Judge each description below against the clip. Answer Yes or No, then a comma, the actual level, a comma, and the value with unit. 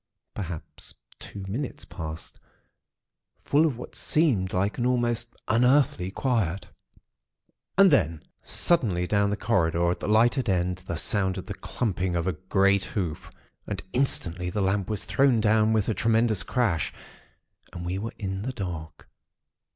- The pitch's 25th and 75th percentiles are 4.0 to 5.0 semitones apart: Yes, average, 4.7 semitones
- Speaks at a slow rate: No, average, 145 wpm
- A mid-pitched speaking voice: No, low, 100 Hz